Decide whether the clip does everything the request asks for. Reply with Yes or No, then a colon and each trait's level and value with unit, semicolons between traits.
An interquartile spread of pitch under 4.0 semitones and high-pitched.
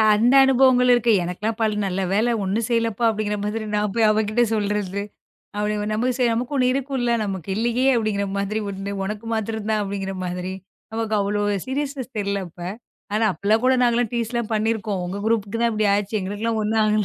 Yes: narrow, 2.5 semitones; high, 215 Hz